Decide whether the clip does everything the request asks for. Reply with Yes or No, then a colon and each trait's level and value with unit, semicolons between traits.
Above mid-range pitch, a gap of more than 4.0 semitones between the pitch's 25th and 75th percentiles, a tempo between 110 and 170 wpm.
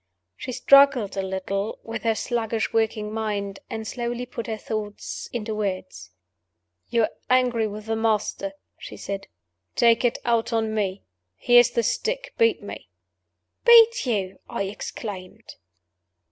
No: high, 225 Hz; average, 2.8 semitones; slow, 135 wpm